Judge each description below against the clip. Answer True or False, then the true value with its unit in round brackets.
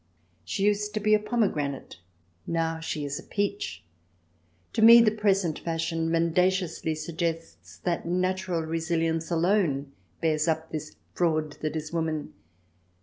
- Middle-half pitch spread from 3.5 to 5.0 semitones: False (3.0 semitones)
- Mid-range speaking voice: True (165 Hz)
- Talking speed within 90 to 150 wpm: True (135 wpm)